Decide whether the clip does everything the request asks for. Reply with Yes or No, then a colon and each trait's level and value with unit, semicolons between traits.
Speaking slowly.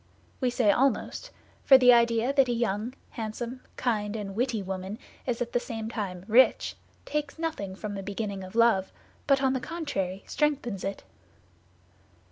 No: average, 160 wpm